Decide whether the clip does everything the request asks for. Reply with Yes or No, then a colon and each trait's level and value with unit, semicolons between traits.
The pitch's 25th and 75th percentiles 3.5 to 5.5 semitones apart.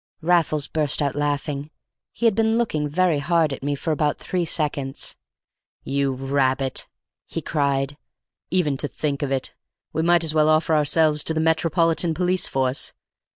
No: average, 2.9 semitones